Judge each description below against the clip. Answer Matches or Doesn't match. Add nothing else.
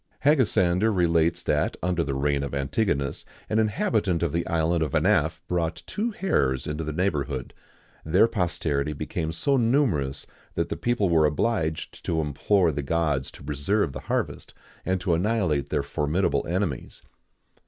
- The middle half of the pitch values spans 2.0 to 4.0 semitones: Doesn't match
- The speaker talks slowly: Doesn't match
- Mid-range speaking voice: Doesn't match